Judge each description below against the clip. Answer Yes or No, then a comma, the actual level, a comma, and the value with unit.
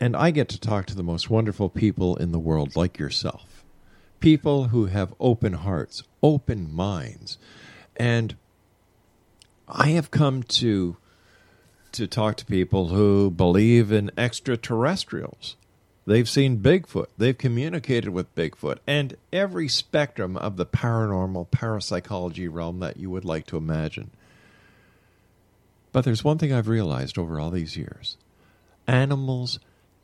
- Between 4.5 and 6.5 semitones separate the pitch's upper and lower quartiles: Yes, average, 5.2 semitones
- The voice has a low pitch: Yes, low, 110 Hz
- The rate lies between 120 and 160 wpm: Yes, slow, 135 wpm